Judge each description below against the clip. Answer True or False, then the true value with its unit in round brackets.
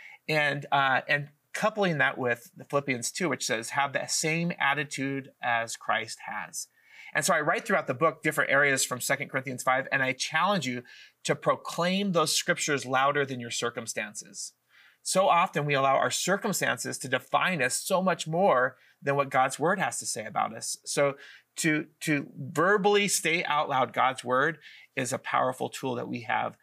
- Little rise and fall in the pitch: False (4.3 semitones)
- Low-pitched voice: False (145 Hz)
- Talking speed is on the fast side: False (180 wpm)